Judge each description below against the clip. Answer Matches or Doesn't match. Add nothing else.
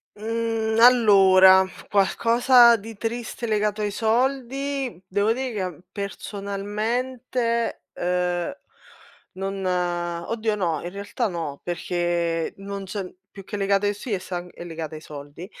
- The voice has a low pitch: Doesn't match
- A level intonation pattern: Doesn't match